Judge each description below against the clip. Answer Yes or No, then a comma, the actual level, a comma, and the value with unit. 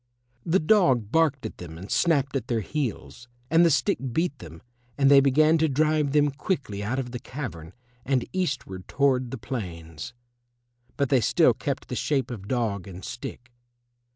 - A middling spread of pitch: No, wide, 6.0 semitones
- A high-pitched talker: No, low, 130 Hz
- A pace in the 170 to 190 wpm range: Yes, average, 175 wpm